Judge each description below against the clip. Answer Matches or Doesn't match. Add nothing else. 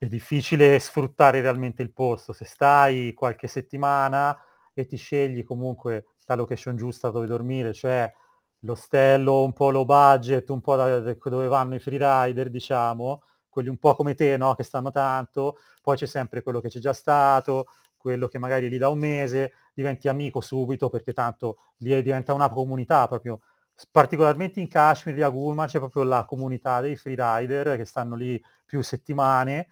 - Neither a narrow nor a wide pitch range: Doesn't match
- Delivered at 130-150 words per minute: Doesn't match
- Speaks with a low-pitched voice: Matches